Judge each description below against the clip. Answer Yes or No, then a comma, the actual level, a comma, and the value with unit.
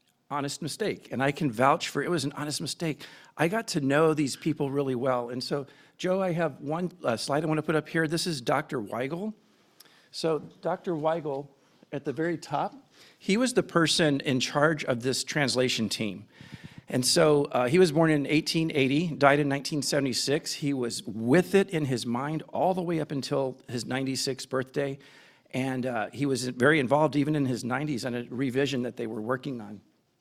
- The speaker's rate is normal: Yes, average, 195 wpm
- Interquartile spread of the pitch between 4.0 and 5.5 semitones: No, average, 3.4 semitones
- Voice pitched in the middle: Yes, medium, 145 Hz